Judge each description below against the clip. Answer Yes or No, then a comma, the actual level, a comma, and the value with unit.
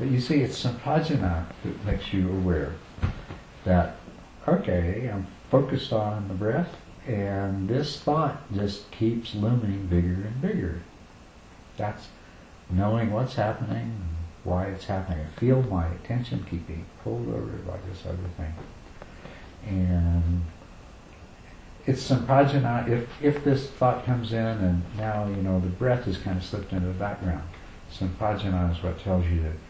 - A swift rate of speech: No, average, 150 wpm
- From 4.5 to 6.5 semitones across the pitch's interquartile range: Yes, average, 5.0 semitones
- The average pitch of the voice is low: Yes, low, 100 Hz